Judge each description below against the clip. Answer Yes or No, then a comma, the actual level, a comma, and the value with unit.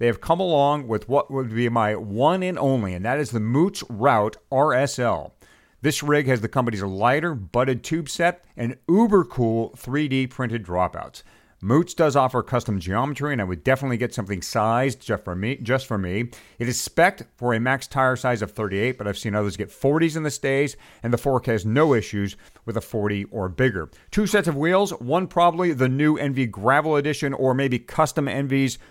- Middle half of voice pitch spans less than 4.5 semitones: No, average, 4.8 semitones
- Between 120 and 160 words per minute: No, average, 200 wpm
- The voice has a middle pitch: No, low, 130 Hz